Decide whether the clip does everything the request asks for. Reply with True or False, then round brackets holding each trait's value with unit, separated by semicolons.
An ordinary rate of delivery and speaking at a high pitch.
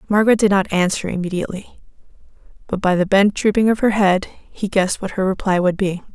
True (195 wpm; 195 Hz)